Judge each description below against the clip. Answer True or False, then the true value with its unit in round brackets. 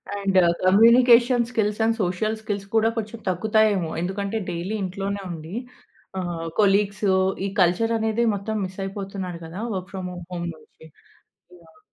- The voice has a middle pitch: False (200 Hz)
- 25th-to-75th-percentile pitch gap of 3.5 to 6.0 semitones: False (3.1 semitones)